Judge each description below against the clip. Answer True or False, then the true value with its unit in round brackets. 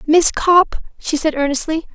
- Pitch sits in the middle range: False (315 Hz)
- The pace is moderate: True (155 wpm)